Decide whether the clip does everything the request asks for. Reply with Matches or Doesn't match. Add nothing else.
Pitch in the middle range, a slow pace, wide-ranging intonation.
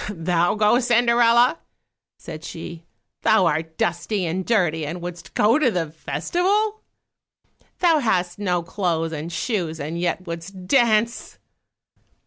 Matches